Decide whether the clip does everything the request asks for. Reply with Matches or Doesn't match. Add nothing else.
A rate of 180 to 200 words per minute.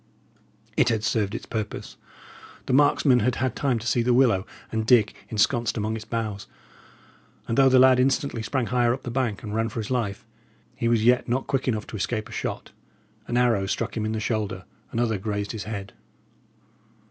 Matches